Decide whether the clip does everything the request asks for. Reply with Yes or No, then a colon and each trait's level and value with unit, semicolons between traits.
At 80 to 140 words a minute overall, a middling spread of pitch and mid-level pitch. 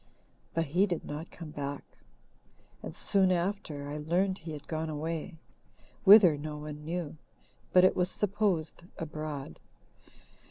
Yes: slow, 135 wpm; average, 3.4 semitones; medium, 160 Hz